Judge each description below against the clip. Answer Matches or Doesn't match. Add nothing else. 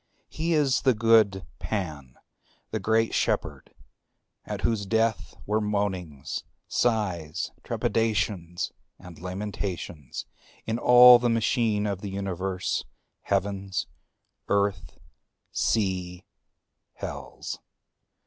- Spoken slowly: Matches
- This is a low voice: Matches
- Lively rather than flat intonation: Doesn't match